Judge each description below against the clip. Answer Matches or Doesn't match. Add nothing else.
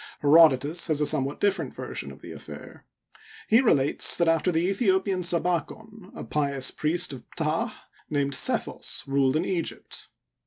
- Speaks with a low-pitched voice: Doesn't match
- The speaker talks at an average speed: Matches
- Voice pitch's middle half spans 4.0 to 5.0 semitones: Matches